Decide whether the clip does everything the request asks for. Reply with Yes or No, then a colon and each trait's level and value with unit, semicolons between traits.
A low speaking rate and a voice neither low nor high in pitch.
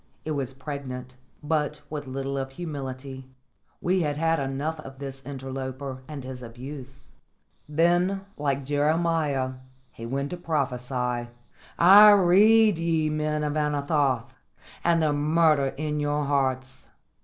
Yes: slow, 130 wpm; medium, 145 Hz